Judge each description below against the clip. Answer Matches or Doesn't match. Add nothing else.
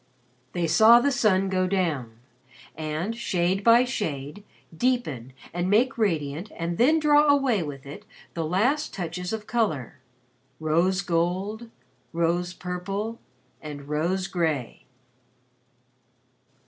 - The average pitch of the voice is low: Doesn't match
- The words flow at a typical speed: Doesn't match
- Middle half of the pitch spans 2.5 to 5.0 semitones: Doesn't match